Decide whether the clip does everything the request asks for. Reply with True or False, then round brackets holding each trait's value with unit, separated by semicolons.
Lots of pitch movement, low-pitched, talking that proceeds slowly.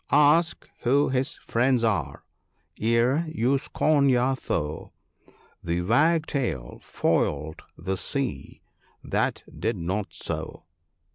True (8.0 semitones; 120 Hz; 115 wpm)